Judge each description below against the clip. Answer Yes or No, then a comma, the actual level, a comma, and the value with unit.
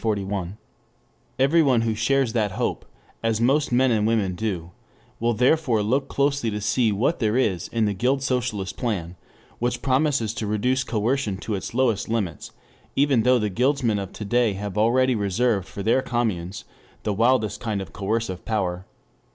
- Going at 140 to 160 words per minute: No, average, 170 wpm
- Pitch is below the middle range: Yes, low, 115 Hz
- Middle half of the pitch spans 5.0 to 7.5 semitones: No, average, 3.6 semitones